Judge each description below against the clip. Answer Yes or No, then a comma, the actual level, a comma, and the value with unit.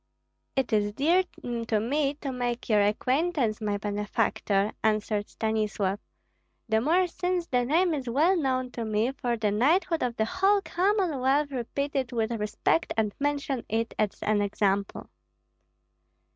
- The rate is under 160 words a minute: Yes, average, 145 wpm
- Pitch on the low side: No, high, 245 Hz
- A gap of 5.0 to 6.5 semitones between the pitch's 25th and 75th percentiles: Yes, wide, 5.5 semitones